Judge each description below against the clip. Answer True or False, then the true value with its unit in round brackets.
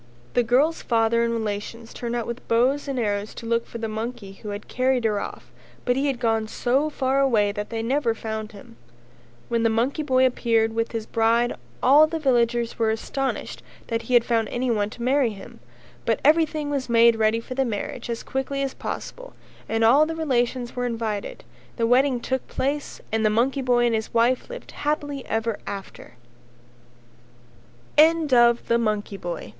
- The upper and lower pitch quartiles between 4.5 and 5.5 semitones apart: False (2.8 semitones)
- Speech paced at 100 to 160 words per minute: False (180 wpm)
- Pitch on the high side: True (235 Hz)